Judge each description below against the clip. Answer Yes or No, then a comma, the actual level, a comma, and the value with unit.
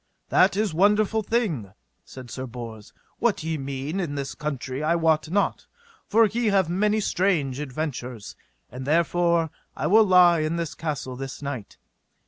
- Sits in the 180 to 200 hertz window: No, medium, 160 Hz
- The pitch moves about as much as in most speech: No, wide, 6.2 semitones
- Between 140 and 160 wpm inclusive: Yes, average, 155 wpm